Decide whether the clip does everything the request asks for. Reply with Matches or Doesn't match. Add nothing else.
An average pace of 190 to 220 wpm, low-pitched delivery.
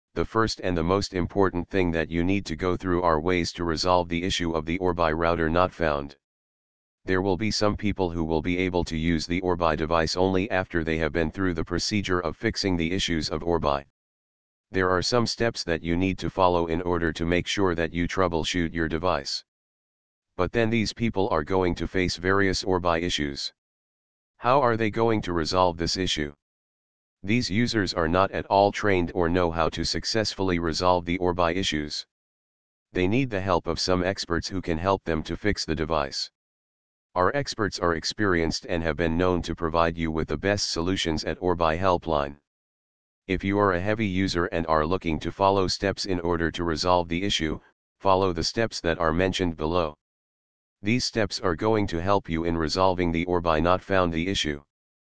Matches